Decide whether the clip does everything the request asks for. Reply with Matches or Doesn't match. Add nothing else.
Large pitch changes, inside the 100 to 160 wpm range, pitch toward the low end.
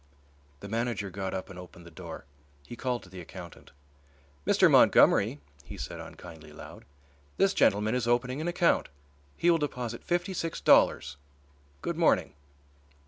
Matches